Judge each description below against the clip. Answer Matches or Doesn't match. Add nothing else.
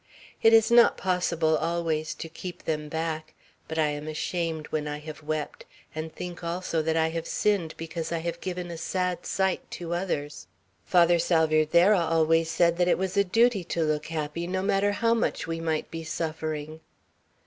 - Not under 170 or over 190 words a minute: Matches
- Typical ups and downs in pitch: Doesn't match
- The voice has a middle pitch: Matches